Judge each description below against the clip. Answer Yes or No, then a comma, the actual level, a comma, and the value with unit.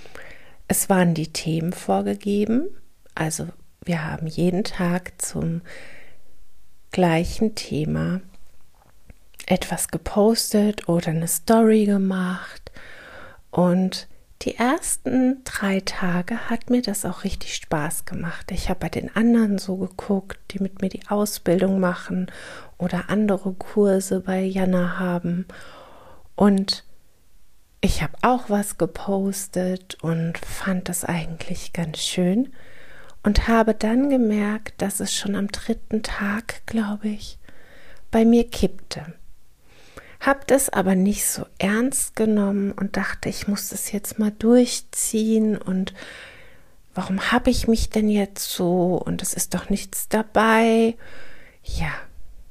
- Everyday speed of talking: No, slow, 120 wpm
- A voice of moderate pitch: No, high, 195 Hz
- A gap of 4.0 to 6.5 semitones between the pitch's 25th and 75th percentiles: No, average, 3.5 semitones